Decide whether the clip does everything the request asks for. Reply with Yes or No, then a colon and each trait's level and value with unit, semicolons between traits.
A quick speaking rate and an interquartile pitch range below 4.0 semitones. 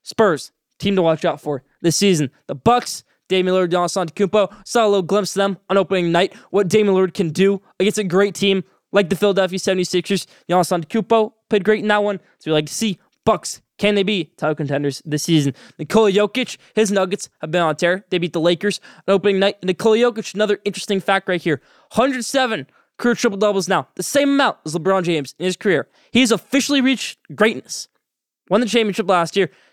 Yes: fast, 210 wpm; average, 3.3 semitones